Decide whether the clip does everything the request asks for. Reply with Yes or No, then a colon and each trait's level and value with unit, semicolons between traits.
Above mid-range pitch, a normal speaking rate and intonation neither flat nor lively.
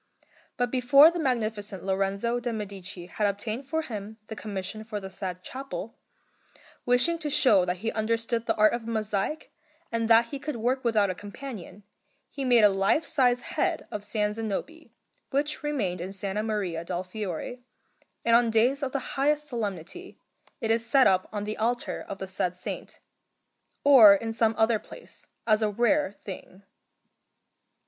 Yes: high, 220 Hz; average, 170 wpm; average, 3.8 semitones